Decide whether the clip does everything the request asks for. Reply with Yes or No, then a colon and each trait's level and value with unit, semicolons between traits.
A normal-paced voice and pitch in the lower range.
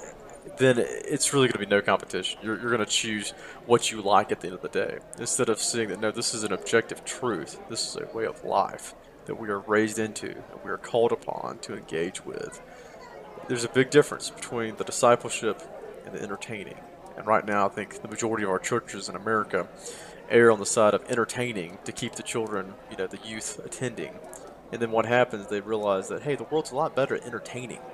No: fast, 220 wpm; low, 115 Hz